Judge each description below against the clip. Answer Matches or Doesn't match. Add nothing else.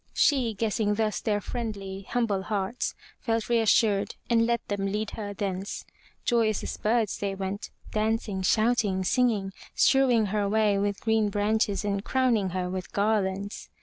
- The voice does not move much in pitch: Matches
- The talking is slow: Doesn't match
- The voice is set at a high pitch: Matches